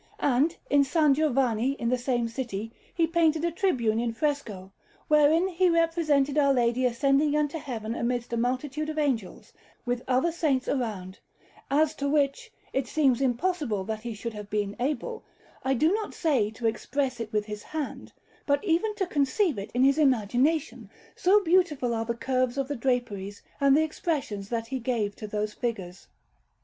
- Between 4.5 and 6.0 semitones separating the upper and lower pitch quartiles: Yes, average, 4.8 semitones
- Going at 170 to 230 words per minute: Yes, average, 175 wpm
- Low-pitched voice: No, very high, 265 Hz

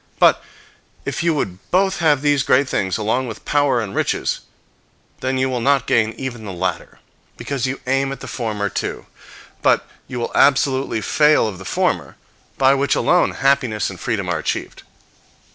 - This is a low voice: Yes, low, 130 Hz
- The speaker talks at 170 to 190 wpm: Yes, average, 175 wpm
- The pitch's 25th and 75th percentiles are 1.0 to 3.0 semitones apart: No, average, 4.2 semitones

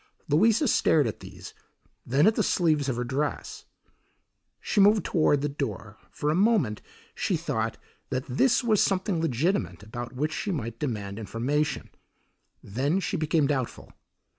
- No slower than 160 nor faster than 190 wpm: No, average, 150 wpm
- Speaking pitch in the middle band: Yes, medium, 145 Hz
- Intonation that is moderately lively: No, wide, 7.1 semitones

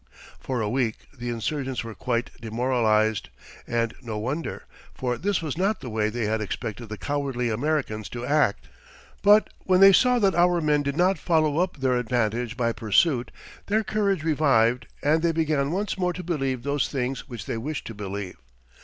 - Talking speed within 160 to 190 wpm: Yes, average, 180 wpm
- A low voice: Yes, low, 130 Hz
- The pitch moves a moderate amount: No, wide, 5.7 semitones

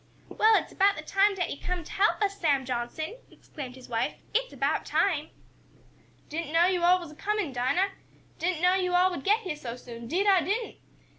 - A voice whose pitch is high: Yes, very high, 355 Hz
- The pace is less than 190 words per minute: No, fast, 205 wpm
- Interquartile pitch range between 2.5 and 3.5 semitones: No, average, 5.1 semitones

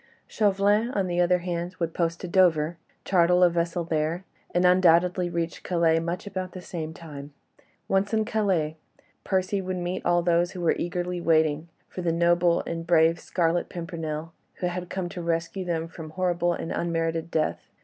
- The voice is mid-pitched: Yes, medium, 175 Hz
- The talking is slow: No, average, 175 wpm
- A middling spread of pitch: No, narrow, 1.6 semitones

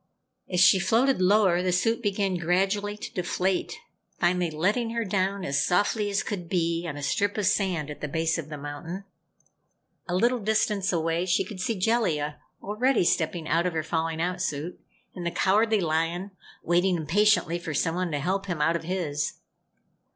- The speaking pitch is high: No, medium, 180 Hz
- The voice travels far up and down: No, average, 3.6 semitones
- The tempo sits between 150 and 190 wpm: Yes, average, 180 wpm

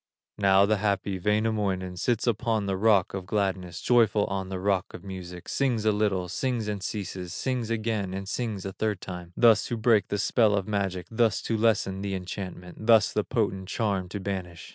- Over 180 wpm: Yes, average, 190 wpm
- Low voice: Yes, low, 100 Hz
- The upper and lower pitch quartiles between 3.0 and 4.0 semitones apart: No, narrow, 2.6 semitones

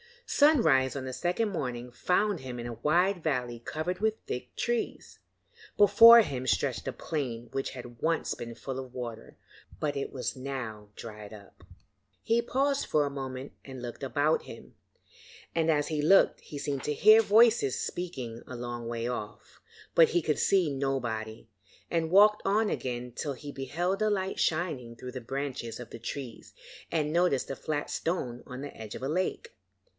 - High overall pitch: No, medium, 140 Hz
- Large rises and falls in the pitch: Yes, wide, 6.2 semitones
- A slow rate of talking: No, average, 175 wpm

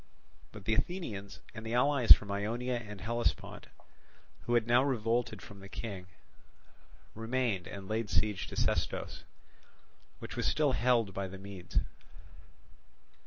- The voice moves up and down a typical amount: Yes, average, 3.2 semitones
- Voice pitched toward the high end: No, low, 110 Hz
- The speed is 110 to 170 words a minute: Yes, slow, 135 wpm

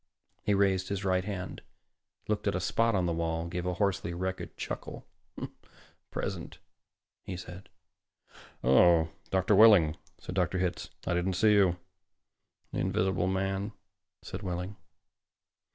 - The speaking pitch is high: No, very low, 95 Hz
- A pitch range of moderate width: No, narrow, 1.9 semitones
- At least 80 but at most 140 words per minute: Yes, slow, 135 wpm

